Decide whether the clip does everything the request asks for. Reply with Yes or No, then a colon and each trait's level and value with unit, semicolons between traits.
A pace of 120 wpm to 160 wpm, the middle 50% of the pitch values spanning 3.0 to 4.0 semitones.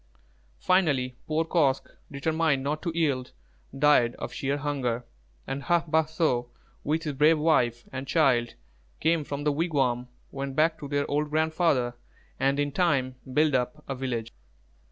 Yes: average, 155 wpm; average, 3.3 semitones